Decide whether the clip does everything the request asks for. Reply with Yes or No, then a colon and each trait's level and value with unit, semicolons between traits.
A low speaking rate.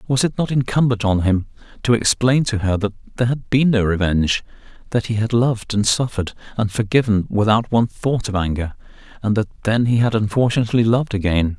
No: average, 185 wpm